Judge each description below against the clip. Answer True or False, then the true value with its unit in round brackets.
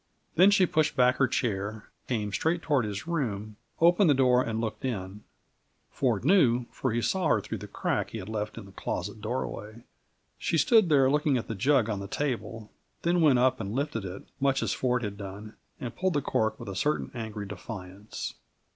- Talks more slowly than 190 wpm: False (200 wpm)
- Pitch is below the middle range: True (120 Hz)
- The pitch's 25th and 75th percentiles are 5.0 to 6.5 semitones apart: True (5.5 semitones)